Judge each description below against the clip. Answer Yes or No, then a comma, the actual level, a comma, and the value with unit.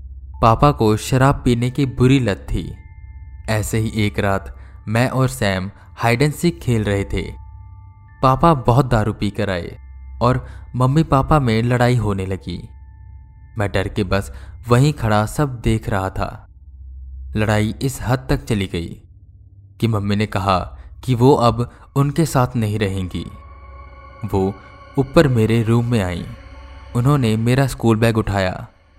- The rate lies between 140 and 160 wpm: Yes, average, 150 wpm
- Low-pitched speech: Yes, low, 105 Hz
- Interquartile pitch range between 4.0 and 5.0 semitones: Yes, average, 4.7 semitones